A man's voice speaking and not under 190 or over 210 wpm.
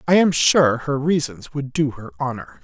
Yes: male; fast, 205 wpm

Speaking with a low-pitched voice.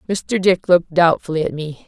No: medium, 170 Hz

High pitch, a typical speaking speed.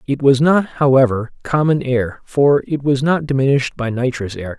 No: low, 135 Hz; average, 185 wpm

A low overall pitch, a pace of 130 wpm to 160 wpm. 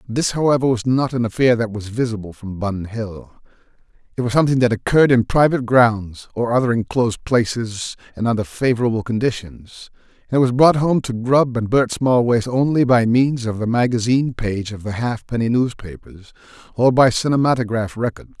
No: low, 120 Hz; average, 175 wpm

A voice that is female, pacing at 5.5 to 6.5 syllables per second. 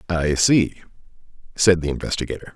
No: male; 5.7 syllables/s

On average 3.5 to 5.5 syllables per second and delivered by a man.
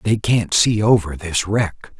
Yes: 3.8 syllables/s; male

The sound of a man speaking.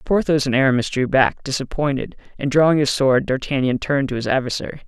Yes: male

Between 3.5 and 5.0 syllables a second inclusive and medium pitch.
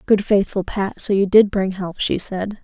No: 4.5 syllables/s; high, 195 Hz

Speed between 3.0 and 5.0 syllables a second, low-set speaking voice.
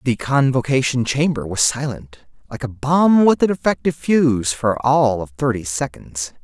Yes: 4.6 syllables/s; low, 130 Hz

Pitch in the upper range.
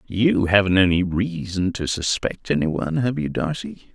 No: low, 105 Hz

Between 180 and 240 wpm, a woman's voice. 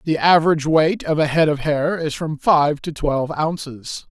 No: average, 200 wpm; male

